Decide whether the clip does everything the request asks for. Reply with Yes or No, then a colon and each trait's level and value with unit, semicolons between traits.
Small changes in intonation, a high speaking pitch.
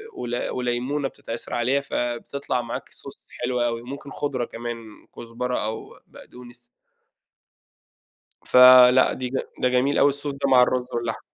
No: narrow, 1.7 semitones; low, 125 Hz